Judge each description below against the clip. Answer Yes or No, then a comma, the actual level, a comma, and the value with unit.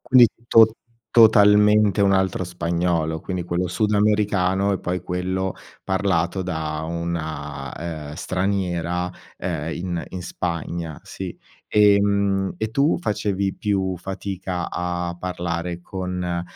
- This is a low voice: Yes, very low, 90 Hz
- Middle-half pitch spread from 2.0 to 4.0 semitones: Yes, average, 2.7 semitones